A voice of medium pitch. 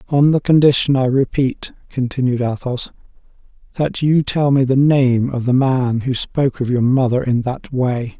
No: low, 130 Hz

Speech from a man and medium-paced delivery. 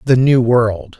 Yes: male; average, 180 wpm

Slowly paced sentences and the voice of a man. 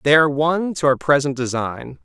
No: fast, 205 wpm; male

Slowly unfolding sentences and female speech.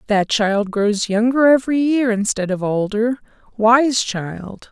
Yes: slow, 125 wpm; female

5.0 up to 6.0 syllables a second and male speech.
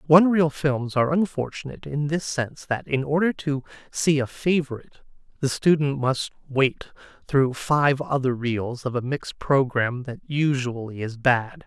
No: 4.8 syllables/s; male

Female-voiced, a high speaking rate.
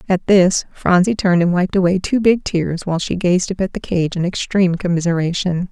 Yes: female; fast, 210 wpm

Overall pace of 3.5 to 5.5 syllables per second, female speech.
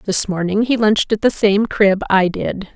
Yes: 4.8 syllables/s; female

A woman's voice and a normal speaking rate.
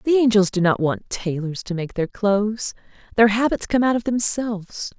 Yes: female; average, 195 wpm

